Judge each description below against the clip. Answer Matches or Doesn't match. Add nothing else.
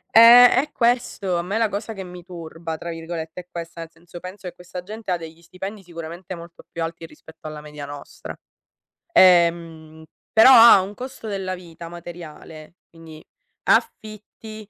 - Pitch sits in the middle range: Matches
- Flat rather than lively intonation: Doesn't match